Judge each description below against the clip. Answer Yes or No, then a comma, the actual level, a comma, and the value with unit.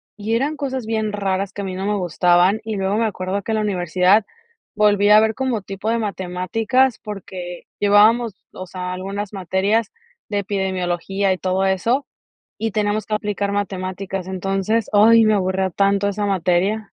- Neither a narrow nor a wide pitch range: No, narrow, 2.3 semitones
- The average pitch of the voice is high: Yes, high, 200 Hz